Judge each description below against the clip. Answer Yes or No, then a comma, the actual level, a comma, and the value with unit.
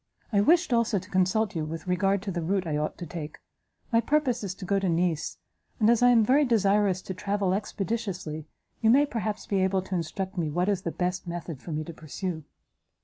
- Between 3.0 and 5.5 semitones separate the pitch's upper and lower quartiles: Yes, average, 3.7 semitones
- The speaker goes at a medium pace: No, fast, 220 wpm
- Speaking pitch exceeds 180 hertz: Yes, high, 190 Hz